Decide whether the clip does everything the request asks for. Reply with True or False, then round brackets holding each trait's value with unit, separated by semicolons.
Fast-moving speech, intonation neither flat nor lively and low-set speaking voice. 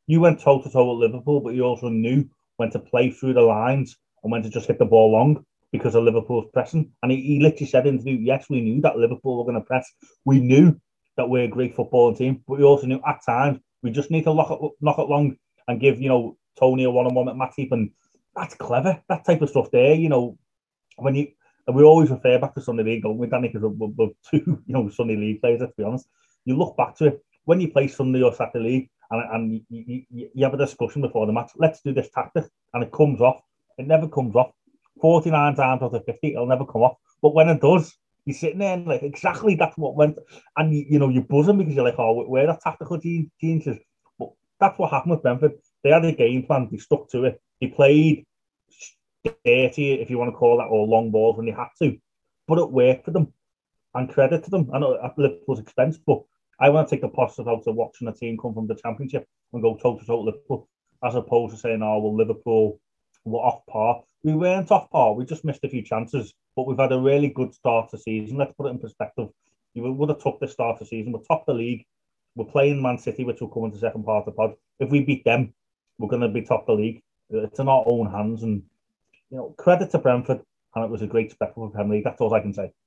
True (250 wpm; 4.1 semitones; 130 Hz)